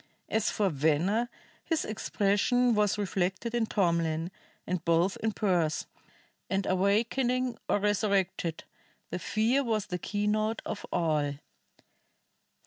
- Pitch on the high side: Yes, high, 200 Hz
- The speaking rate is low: Yes, slow, 110 wpm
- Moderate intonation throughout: Yes, average, 3.9 semitones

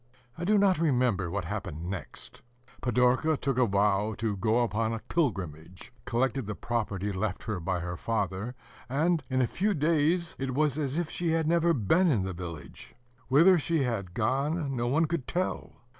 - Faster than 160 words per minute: Yes, average, 180 wpm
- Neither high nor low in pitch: No, low, 125 Hz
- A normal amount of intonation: No, wide, 7.7 semitones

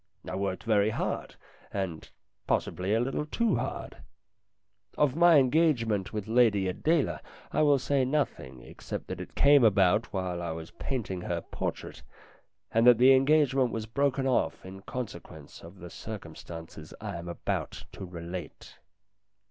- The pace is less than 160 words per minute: Yes, average, 150 wpm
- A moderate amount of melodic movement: No, wide, 7.0 semitones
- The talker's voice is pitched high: No, low, 110 Hz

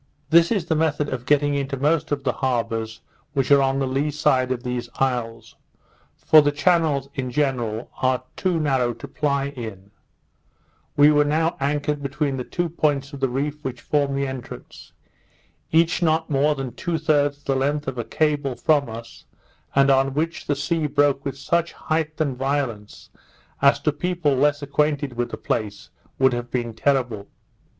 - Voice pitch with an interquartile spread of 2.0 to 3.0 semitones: Yes, narrow, 2.6 semitones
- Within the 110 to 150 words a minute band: No, average, 175 wpm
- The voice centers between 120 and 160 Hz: Yes, medium, 140 Hz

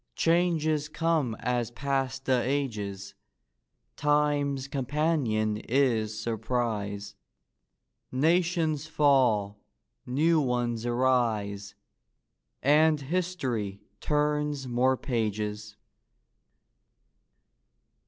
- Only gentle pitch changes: No, average, 5.2 semitones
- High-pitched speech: No, low, 130 Hz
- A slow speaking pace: Yes, slow, 65 wpm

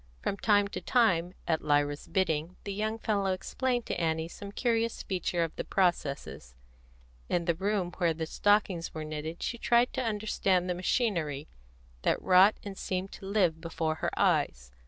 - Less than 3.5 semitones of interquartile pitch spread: No, average, 4.2 semitones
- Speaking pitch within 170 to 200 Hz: Yes, medium, 185 Hz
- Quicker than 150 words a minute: Yes, average, 170 wpm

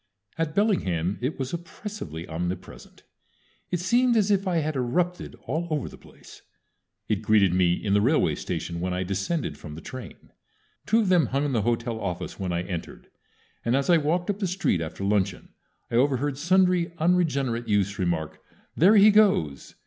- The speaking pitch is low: Yes, low, 130 Hz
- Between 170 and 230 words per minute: Yes, average, 180 wpm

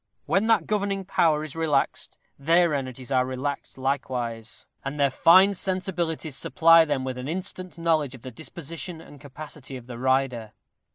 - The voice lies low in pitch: No, medium, 150 Hz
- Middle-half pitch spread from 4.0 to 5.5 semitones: Yes, average, 4.4 semitones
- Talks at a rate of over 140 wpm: Yes, average, 160 wpm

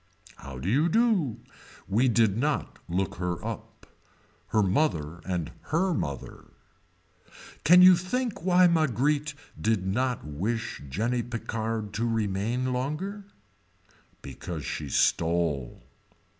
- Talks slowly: Yes, slow, 115 wpm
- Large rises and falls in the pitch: Yes, wide, 8.5 semitones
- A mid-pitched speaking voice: No, low, 115 Hz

